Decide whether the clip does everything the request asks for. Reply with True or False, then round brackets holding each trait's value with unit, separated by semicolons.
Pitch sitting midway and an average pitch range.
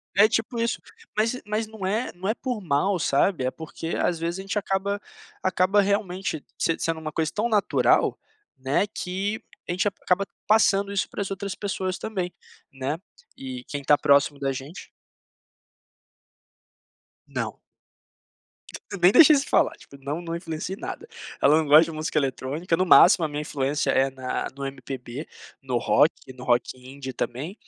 False (170 Hz; 6.1 semitones)